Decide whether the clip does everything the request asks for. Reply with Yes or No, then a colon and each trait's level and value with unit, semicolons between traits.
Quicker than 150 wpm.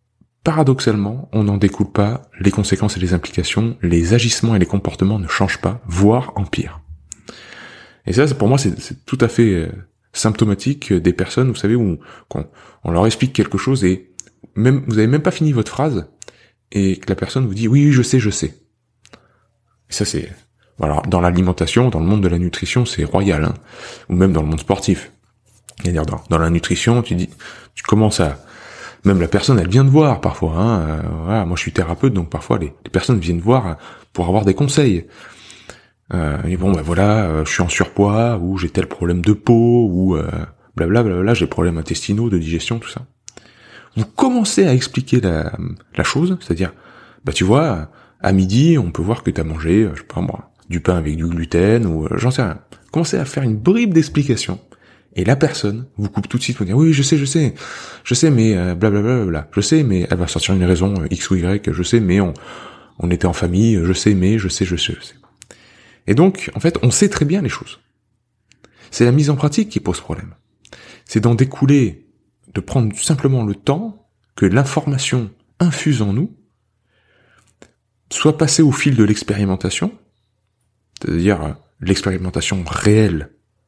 Yes: average, 200 wpm